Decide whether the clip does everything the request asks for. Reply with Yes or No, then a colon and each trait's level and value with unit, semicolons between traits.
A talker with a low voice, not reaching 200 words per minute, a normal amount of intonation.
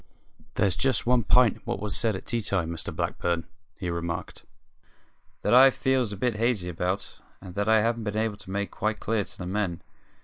No: low, 105 Hz; fast, 205 wpm; average, 3.9 semitones